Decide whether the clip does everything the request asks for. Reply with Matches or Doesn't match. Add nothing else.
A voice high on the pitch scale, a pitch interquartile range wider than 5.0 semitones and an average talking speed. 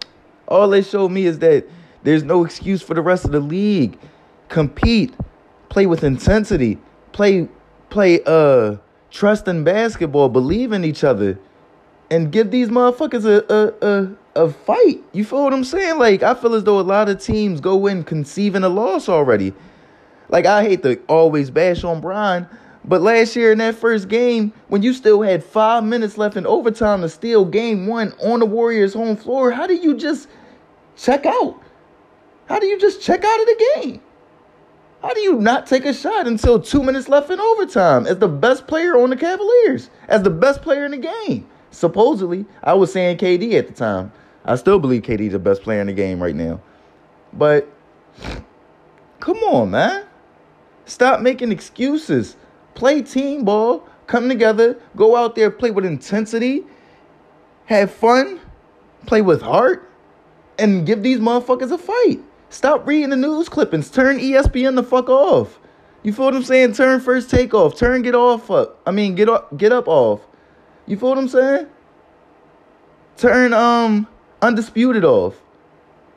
Matches